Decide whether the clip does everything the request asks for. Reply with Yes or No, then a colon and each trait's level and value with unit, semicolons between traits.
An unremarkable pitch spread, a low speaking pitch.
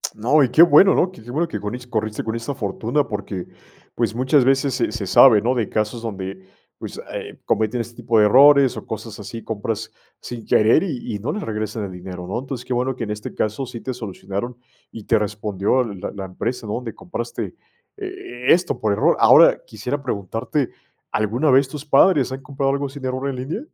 Yes: average, 4.1 semitones; low, 120 Hz